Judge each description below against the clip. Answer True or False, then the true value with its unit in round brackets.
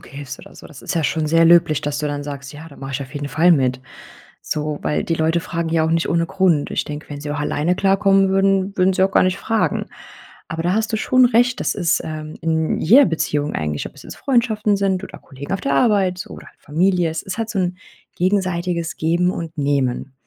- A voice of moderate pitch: True (165 Hz)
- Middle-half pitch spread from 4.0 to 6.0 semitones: True (4.5 semitones)